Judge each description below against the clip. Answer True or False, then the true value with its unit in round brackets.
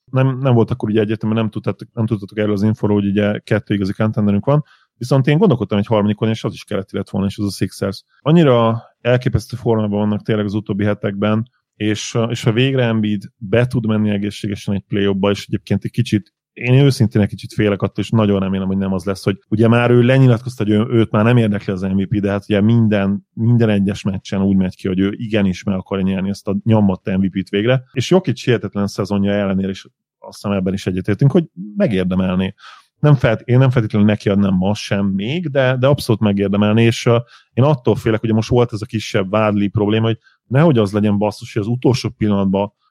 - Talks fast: True (210 wpm)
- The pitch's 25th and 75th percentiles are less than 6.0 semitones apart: True (2.8 semitones)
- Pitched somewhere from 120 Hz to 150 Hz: False (105 Hz)